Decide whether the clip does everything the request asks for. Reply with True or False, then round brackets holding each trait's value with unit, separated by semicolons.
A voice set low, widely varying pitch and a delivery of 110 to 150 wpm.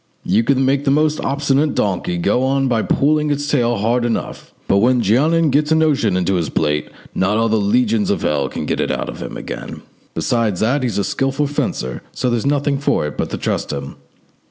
False (125 Hz; 5.8 semitones; 205 wpm)